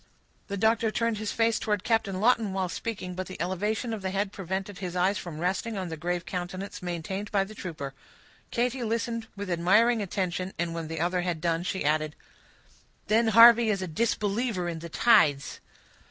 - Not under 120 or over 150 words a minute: No, average, 185 wpm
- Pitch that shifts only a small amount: No, average, 3.9 semitones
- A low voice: No, high, 190 Hz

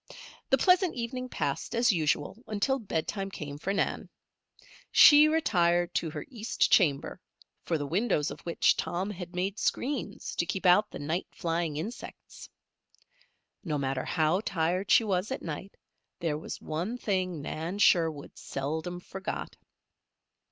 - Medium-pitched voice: Yes, medium, 180 Hz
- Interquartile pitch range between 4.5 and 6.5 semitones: Yes, average, 5.0 semitones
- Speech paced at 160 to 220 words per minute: No, average, 145 wpm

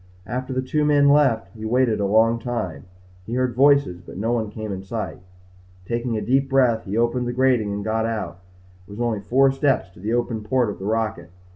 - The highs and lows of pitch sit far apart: No, average, 3.2 semitones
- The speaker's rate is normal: No, fast, 220 wpm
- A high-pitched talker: No, low, 115 Hz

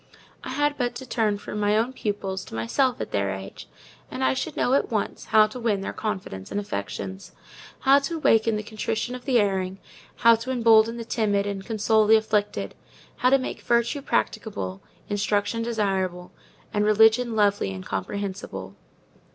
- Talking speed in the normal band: Yes, average, 175 wpm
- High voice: Yes, high, 210 Hz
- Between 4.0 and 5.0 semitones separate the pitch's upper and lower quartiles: No, average, 3.4 semitones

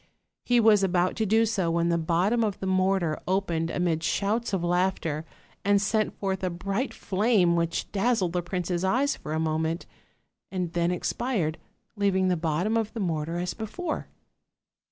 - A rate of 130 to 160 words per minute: No, average, 170 wpm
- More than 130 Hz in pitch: Yes, medium, 185 Hz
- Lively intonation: No, average, 3.6 semitones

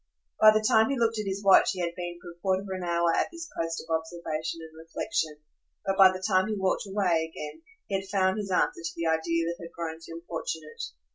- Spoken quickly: Yes, fast, 240 wpm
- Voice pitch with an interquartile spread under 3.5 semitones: Yes, average, 2.9 semitones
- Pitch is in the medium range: Yes, medium, 175 Hz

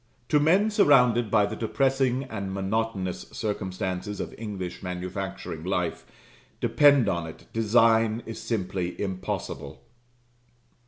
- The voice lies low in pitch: Yes, low, 105 Hz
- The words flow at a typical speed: No, slow, 110 wpm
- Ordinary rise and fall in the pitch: Yes, average, 4.4 semitones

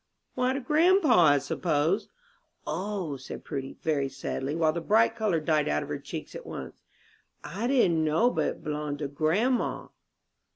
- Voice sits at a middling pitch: Yes, medium, 165 Hz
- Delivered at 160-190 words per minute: Yes, average, 165 wpm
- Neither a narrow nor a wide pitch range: No, wide, 7.2 semitones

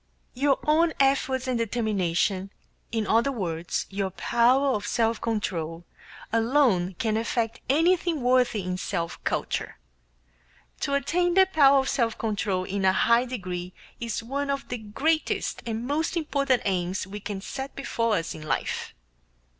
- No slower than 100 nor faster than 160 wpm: Yes, average, 145 wpm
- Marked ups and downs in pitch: Yes, wide, 5.9 semitones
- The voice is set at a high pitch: Yes, high, 230 Hz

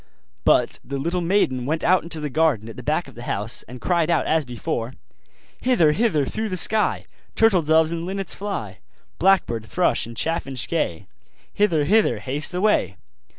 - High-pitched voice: No, medium, 160 Hz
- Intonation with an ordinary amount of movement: No, wide, 6.3 semitones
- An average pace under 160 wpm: No, average, 175 wpm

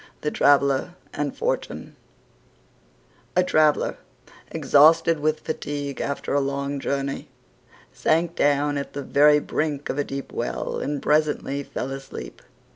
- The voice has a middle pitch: Yes, medium, 145 Hz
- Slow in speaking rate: Yes, slow, 125 wpm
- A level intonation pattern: Yes, narrow, 1.6 semitones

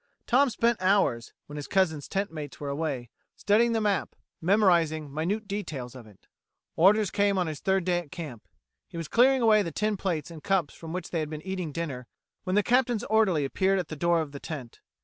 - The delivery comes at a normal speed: No, fast, 210 wpm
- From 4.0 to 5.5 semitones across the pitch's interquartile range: Yes, average, 5.1 semitones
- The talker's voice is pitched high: No, medium, 175 Hz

